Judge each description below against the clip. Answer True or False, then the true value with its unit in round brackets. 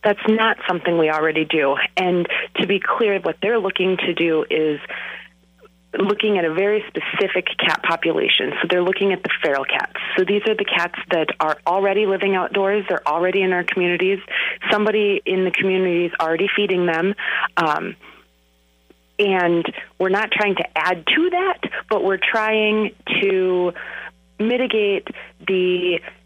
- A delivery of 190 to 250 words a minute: False (155 wpm)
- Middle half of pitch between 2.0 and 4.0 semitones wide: True (2.8 semitones)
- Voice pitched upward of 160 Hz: True (190 Hz)